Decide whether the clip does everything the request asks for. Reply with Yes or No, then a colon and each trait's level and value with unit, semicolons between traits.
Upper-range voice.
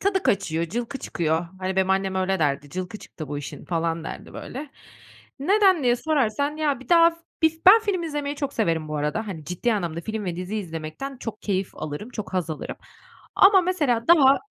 Yes: high, 215 Hz